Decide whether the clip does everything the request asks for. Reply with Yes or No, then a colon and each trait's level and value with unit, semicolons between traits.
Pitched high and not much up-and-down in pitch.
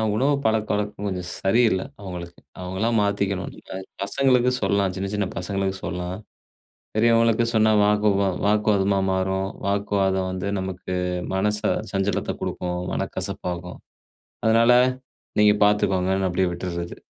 No: low, 100 Hz; narrow, 2.1 semitones